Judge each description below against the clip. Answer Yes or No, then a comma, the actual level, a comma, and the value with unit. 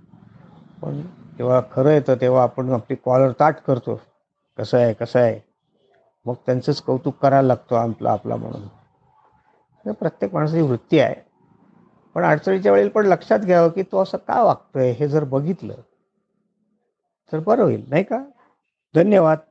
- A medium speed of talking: No, fast, 145 wpm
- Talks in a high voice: No, medium, 140 Hz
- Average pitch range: No, wide, 6.5 semitones